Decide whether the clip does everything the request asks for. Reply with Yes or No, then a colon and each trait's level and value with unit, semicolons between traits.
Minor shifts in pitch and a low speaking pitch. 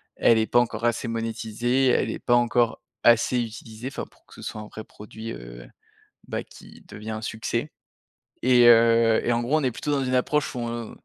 Yes: narrow, 1.7 semitones; low, 115 Hz